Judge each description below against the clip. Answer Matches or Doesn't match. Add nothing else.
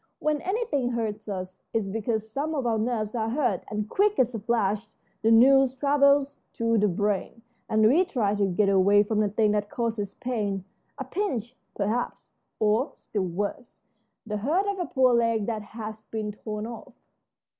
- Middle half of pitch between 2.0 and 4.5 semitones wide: Matches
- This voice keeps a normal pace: Matches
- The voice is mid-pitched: Doesn't match